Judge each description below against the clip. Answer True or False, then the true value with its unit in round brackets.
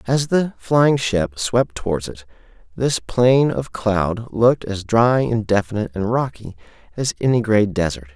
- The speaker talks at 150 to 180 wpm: True (160 wpm)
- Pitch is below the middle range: True (110 Hz)